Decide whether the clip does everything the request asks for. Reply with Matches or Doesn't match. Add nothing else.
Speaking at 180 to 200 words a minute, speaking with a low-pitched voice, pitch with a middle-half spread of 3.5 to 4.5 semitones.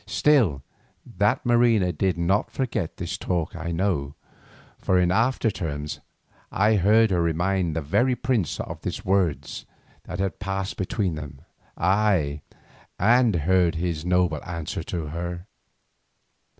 Doesn't match